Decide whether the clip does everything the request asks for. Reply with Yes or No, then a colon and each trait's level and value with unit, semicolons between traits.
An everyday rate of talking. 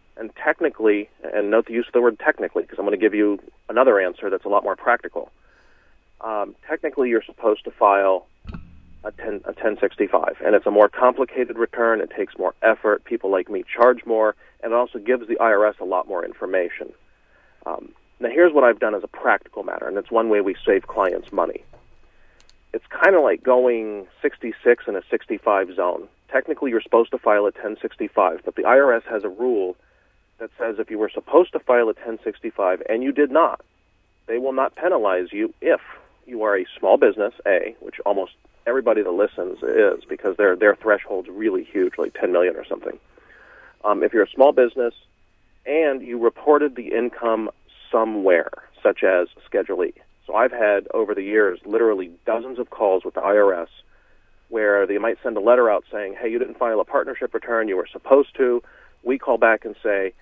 Yes: average, 195 wpm